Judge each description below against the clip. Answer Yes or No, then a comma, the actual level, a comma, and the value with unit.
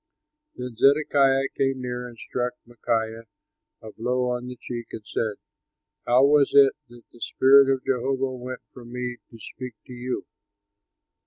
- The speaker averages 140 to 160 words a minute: Yes, average, 155 wpm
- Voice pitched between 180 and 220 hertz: No, low, 125 Hz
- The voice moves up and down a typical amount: No, narrow, 1.9 semitones